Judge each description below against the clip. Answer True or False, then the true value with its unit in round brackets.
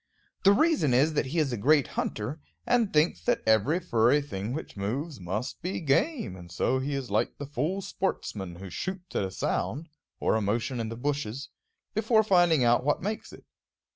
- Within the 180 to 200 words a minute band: True (195 wpm)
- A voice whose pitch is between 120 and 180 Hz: True (140 Hz)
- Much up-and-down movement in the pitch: True (7.4 semitones)